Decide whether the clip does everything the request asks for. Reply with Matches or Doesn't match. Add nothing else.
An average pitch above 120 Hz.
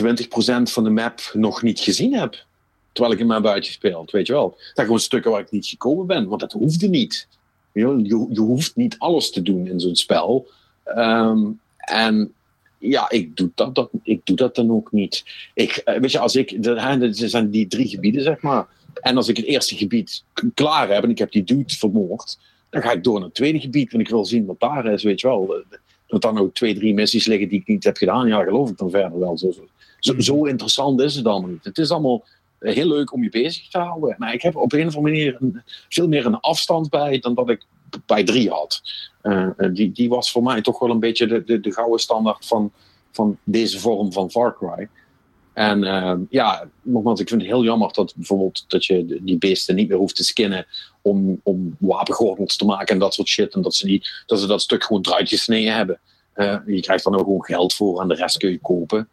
Doesn't match